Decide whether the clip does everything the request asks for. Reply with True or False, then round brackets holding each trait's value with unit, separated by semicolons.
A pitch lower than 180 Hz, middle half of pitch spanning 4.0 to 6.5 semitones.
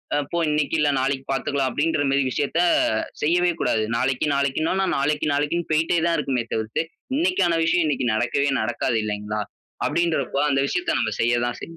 True (140 Hz; 4.8 semitones)